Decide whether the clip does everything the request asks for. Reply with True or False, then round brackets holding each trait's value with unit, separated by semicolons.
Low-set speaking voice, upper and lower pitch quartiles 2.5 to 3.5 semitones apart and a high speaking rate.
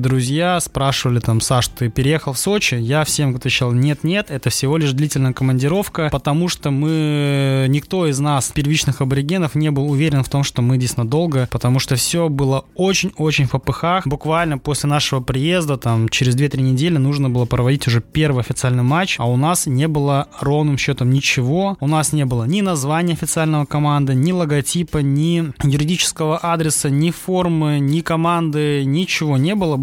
False (145 Hz; 3.0 semitones; 170 wpm)